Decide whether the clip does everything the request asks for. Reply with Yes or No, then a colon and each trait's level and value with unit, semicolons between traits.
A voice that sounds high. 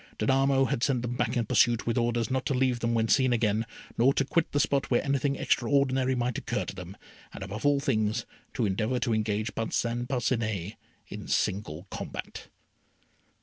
No: low, 120 Hz